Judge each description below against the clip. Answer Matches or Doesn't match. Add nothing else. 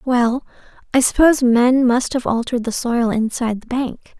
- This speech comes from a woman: Matches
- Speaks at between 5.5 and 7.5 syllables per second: Doesn't match